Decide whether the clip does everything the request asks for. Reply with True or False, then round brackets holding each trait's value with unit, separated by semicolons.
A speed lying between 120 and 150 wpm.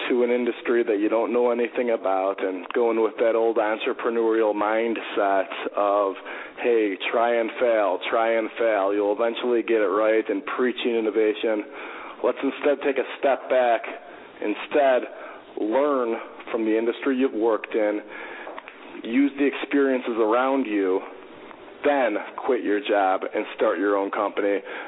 True (145 wpm)